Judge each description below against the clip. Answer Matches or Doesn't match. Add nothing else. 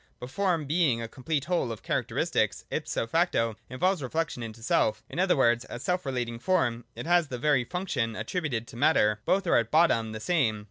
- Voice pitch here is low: Matches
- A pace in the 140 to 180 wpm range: Doesn't match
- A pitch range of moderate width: Doesn't match